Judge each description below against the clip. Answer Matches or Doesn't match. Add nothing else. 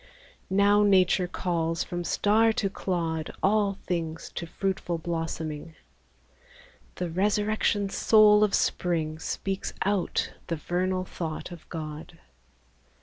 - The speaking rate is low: Matches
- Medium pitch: Matches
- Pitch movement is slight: Doesn't match